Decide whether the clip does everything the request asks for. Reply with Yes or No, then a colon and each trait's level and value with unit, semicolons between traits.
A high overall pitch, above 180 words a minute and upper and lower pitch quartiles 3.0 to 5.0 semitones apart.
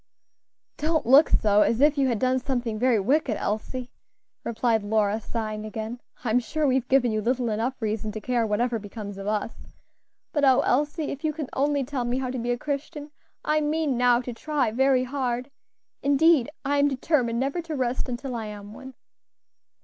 Yes: very high, 250 Hz; average, 190 wpm; average, 3.9 semitones